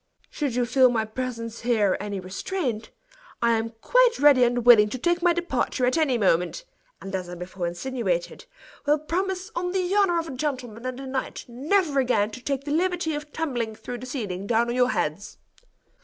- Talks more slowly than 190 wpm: No, average, 195 wpm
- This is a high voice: Yes, very high, 255 Hz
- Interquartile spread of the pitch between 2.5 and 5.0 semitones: No, wide, 5.6 semitones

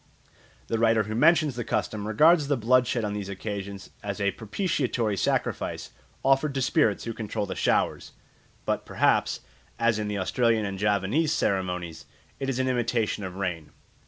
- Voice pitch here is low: Yes, low, 110 Hz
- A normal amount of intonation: Yes, average, 4.0 semitones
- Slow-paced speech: No, average, 165 wpm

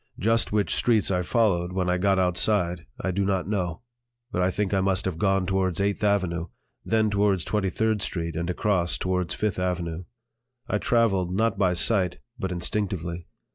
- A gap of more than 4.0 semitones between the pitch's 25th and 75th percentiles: No, narrow, 2.4 semitones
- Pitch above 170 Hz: No, very low, 95 Hz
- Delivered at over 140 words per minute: Yes, average, 180 wpm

